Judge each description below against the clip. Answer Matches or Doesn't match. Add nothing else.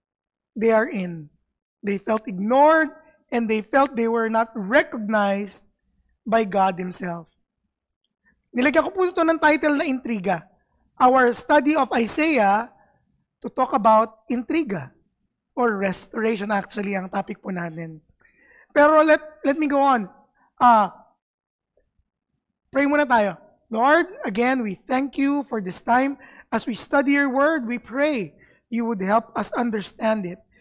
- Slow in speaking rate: Matches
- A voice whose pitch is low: Doesn't match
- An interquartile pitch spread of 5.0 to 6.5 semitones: Matches